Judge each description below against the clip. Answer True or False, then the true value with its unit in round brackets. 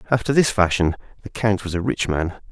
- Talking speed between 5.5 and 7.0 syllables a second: True (5.8 syllables/s)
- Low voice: True (100 Hz)